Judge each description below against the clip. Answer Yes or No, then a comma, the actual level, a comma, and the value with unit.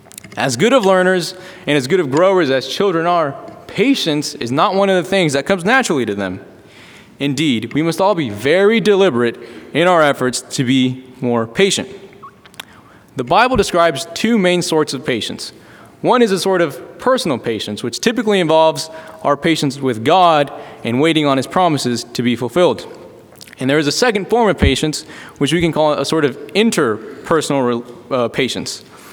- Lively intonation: Yes, wide, 6.1 semitones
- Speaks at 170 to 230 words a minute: Yes, average, 175 wpm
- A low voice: No, medium, 160 Hz